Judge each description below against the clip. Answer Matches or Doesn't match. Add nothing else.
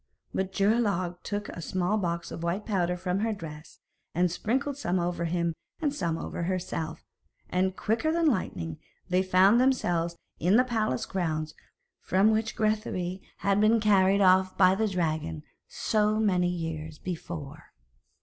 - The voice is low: Doesn't match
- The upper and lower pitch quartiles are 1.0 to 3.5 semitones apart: Doesn't match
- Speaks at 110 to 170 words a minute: Matches